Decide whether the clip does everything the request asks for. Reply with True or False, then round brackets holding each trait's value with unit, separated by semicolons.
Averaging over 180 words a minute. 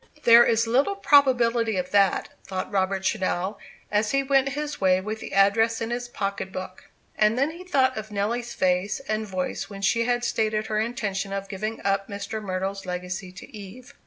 True (190 wpm)